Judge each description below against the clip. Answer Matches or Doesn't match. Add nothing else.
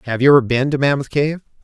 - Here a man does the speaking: Matches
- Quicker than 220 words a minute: Matches